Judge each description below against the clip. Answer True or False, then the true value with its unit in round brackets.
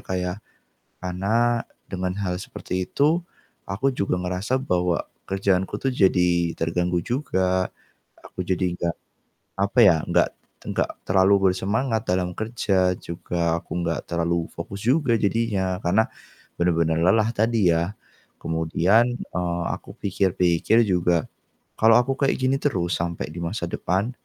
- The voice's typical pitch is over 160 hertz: False (95 Hz)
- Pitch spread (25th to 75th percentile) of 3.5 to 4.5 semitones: True (4.1 semitones)